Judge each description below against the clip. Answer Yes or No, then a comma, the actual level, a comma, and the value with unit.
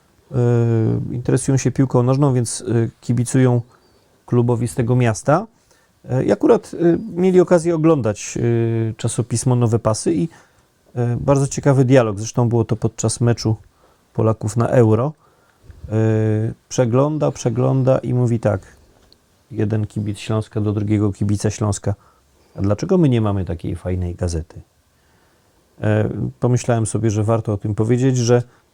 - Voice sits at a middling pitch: No, low, 115 Hz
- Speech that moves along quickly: No, average, 120 wpm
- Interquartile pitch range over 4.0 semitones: No, average, 3.0 semitones